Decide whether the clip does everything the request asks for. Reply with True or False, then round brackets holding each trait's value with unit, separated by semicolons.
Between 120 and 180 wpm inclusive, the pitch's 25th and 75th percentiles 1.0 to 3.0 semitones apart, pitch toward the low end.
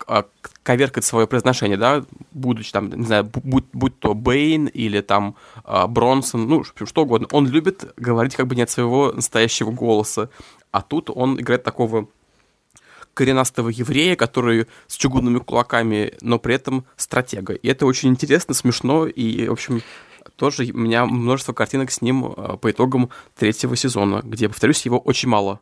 True (160 wpm; 2.7 semitones; 125 Hz)